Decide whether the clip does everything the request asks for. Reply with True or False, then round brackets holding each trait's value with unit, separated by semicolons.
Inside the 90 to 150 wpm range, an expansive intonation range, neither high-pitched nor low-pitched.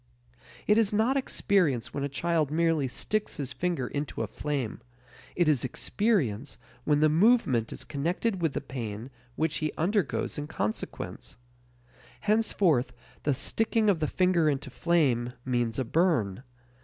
True (145 wpm; 5.8 semitones; 155 Hz)